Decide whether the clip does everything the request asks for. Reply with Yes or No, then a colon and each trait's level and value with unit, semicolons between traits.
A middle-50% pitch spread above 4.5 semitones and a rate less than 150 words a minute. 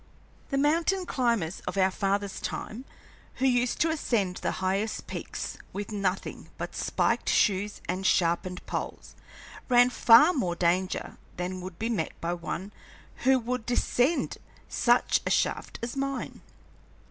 Yes: average, 5.2 semitones; average, 140 wpm